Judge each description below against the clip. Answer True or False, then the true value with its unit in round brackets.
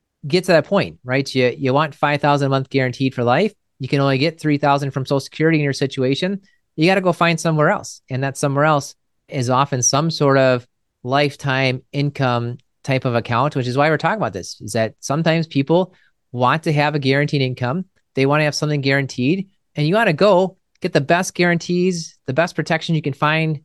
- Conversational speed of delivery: False (220 wpm)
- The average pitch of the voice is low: False (145 Hz)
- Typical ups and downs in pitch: True (3.5 semitones)